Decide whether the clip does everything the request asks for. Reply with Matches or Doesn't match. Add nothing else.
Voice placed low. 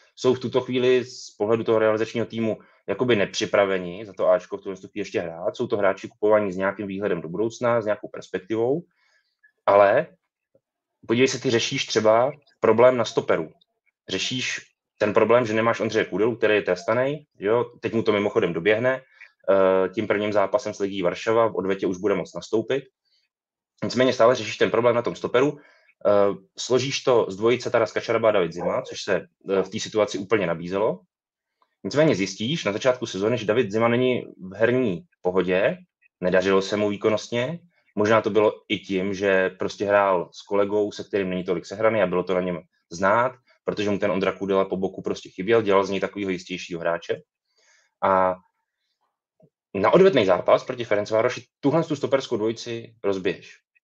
Matches